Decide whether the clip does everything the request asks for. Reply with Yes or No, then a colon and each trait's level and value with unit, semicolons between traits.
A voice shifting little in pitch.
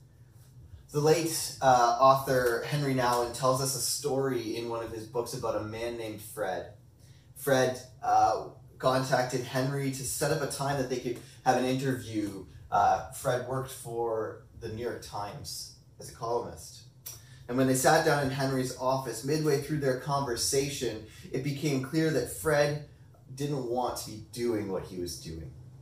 Yes: narrow, 2.1 semitones